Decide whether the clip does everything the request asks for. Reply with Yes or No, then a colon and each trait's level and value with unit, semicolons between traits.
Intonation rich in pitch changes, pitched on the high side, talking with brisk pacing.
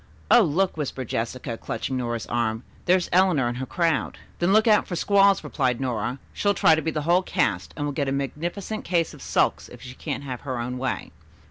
No: wide, 5.9 semitones; medium, 145 Hz; fast, 215 wpm